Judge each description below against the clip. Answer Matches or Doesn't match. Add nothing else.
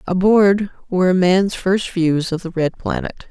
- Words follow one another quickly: Doesn't match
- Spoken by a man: Doesn't match